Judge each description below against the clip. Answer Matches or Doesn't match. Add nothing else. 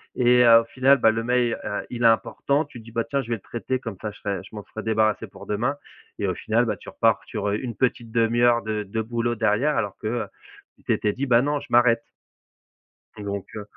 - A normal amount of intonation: Doesn't match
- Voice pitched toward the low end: Matches